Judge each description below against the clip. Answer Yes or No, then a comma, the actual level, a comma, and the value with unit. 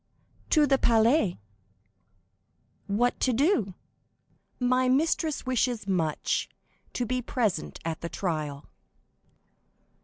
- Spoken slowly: Yes, slow, 95 wpm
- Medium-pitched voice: No, high, 240 Hz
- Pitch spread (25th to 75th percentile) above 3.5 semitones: Yes, wide, 5.5 semitones